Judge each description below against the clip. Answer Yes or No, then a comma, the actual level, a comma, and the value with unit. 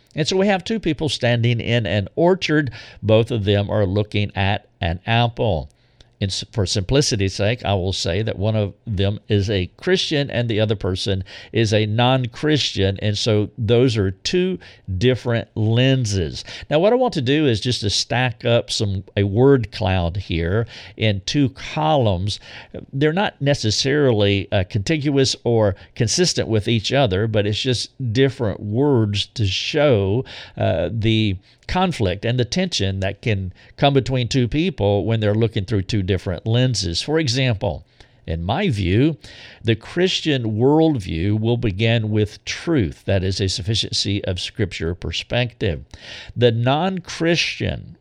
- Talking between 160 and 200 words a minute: No, average, 150 wpm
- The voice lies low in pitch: Yes, low, 110 Hz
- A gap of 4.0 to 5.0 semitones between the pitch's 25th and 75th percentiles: Yes, average, 4.3 semitones